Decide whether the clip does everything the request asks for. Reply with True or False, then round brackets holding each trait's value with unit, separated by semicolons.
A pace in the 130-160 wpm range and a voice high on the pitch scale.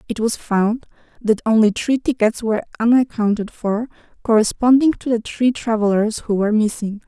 True (155 wpm; 225 Hz)